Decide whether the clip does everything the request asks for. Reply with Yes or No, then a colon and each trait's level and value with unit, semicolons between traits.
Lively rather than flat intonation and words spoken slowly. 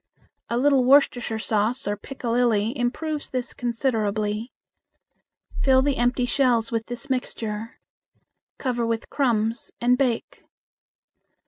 No: narrow, 2.6 semitones; slow, 110 wpm